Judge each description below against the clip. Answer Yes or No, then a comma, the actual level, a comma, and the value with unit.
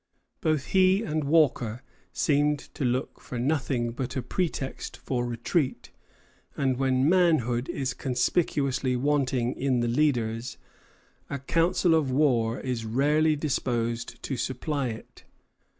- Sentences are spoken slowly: Yes, slow, 125 wpm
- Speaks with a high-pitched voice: No, low, 135 Hz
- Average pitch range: Yes, average, 3.7 semitones